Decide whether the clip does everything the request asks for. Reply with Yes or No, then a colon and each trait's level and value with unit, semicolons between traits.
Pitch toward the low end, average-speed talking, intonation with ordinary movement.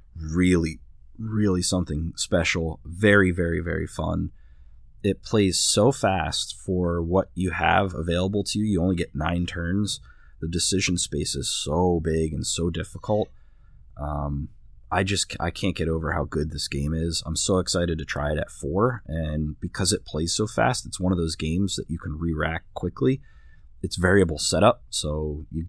Yes: very low, 85 Hz; average, 175 wpm; average, 3.4 semitones